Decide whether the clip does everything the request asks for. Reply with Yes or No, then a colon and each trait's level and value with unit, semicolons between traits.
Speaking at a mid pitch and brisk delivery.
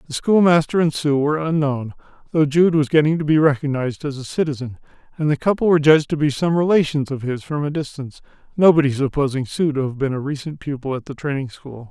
Yes: medium, 145 Hz; fast, 215 wpm